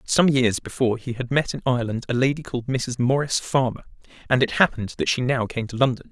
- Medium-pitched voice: No, low, 125 Hz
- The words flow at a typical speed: No, fast, 225 wpm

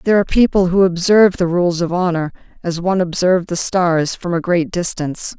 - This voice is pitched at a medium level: Yes, medium, 175 Hz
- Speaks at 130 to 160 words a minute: No, average, 200 wpm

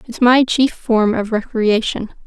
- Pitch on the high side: Yes, high, 230 Hz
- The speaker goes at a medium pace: Yes, average, 160 wpm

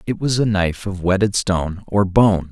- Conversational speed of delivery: No, fast, 215 wpm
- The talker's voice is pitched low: Yes, low, 100 Hz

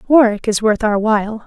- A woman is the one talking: Yes, female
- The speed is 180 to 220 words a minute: Yes, fast, 205 wpm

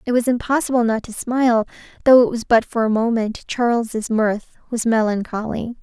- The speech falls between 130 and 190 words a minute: Yes, average, 165 wpm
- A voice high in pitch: Yes, high, 230 Hz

